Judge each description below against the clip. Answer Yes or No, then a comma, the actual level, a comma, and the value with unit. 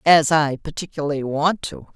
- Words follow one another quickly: No, average, 155 wpm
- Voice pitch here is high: No, medium, 155 Hz